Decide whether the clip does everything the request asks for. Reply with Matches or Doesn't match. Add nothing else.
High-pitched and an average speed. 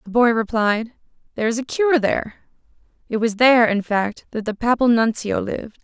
Matches